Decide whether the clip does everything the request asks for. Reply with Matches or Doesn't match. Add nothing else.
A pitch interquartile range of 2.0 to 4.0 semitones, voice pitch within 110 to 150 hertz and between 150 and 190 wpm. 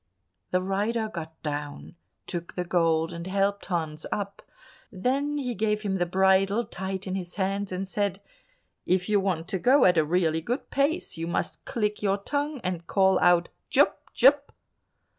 Doesn't match